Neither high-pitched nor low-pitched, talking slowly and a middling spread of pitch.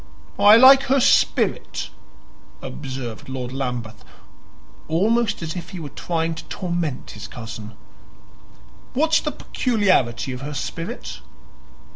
No: medium, 160 Hz; slow, 115 wpm; wide, 8.5 semitones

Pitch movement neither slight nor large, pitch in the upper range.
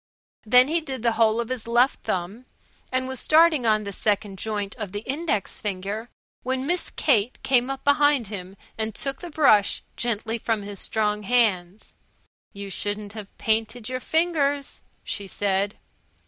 Yes: average, 4.2 semitones; high, 225 Hz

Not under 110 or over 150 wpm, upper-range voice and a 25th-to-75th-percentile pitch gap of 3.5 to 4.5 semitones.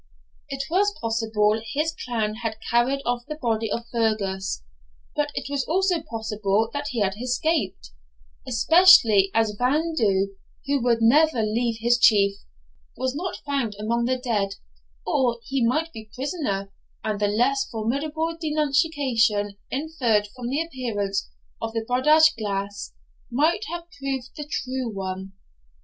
No: average, 140 wpm; high, 240 Hz; average, 5.0 semitones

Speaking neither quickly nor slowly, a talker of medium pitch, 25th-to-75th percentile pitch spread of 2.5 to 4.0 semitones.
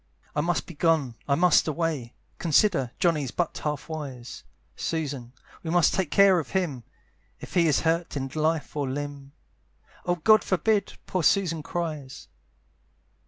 Yes: average, 150 wpm; medium, 160 Hz; average, 3.6 semitones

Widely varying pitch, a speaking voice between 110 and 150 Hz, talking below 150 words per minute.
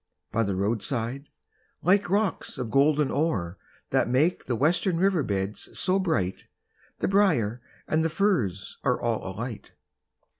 Yes: wide, 8.0 semitones; low, 135 Hz; average, 140 wpm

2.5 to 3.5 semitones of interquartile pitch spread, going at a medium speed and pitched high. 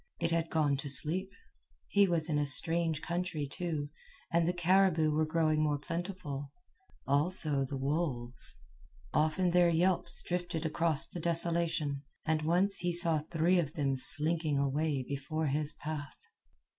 No: average, 2.9 semitones; average, 145 wpm; medium, 160 Hz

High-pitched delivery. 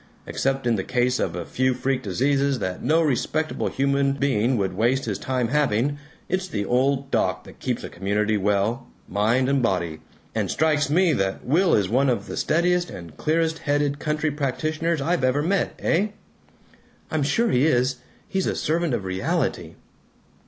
No: low, 135 Hz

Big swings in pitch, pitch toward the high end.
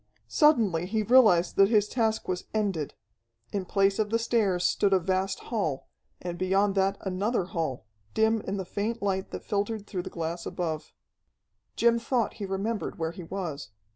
No: average, 3.4 semitones; high, 195 Hz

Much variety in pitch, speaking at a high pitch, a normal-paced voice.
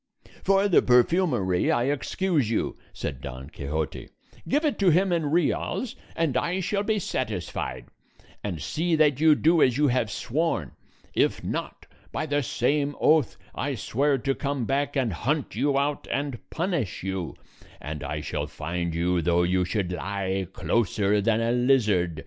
No: wide, 8.8 semitones; low, 130 Hz; average, 160 wpm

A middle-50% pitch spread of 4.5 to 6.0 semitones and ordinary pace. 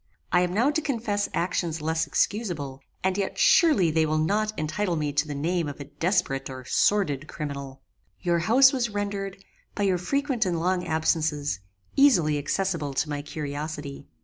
Yes: wide, 5.5 semitones; average, 170 wpm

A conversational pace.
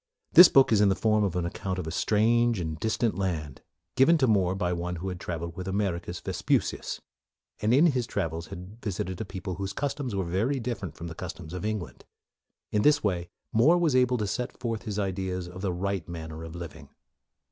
No: fast, 210 wpm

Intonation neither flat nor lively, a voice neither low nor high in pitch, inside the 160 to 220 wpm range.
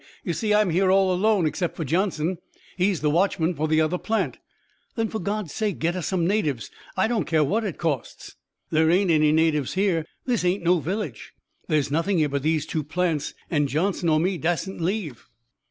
Yes: average, 3.8 semitones; medium, 175 Hz; average, 200 wpm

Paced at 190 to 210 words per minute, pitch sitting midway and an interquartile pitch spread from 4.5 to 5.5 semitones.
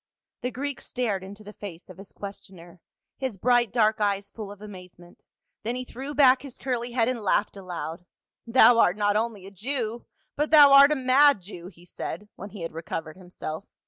No: average, 200 wpm; high, 210 Hz; average, 5.1 semitones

